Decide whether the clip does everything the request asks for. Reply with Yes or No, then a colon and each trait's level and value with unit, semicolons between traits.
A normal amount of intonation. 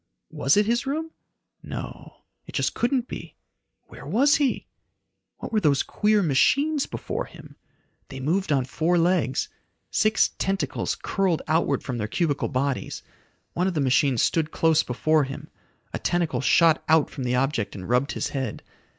No: wide, 6.5 semitones